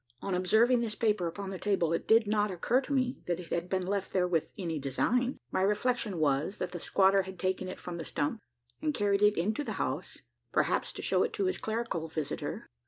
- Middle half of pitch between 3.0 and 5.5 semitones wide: Yes, average, 3.9 semitones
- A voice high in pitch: Yes, high, 195 Hz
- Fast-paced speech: Yes, fast, 225 wpm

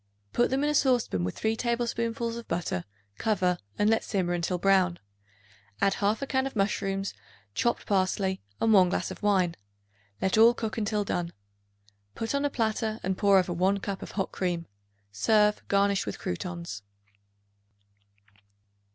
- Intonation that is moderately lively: Yes, average, 3.7 semitones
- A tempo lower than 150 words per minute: No, average, 155 wpm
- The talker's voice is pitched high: Yes, high, 200 Hz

